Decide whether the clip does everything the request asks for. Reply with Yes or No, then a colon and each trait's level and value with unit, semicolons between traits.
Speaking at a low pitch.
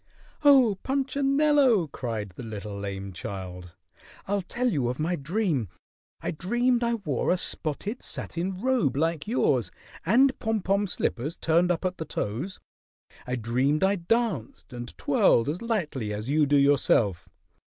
No: medium, 165 Hz